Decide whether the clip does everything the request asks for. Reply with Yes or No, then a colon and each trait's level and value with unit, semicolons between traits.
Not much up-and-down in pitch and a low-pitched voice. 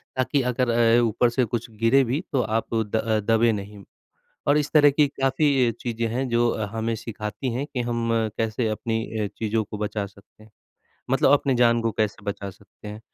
No: average, 3.0 semitones; low, 115 Hz